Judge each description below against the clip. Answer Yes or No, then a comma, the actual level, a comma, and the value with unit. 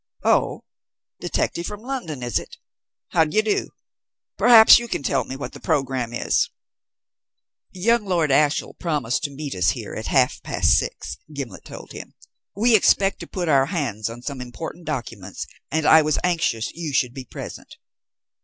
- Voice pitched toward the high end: No, medium, 150 Hz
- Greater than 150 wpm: Yes, average, 165 wpm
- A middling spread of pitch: No, wide, 5.7 semitones